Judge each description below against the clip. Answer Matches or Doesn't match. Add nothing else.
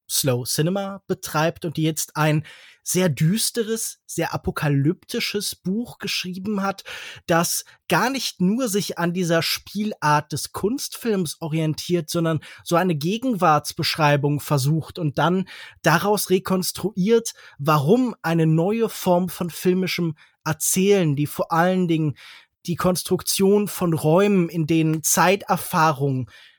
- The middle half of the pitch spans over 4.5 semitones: Doesn't match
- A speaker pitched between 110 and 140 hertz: Doesn't match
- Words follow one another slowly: Matches